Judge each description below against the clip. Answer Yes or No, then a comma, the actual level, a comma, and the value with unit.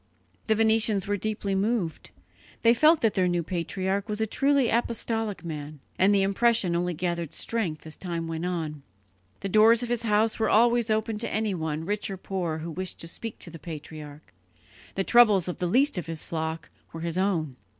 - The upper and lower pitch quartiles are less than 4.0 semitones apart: No, average, 4.9 semitones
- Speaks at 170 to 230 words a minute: Yes, average, 190 wpm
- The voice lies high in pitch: Yes, high, 195 Hz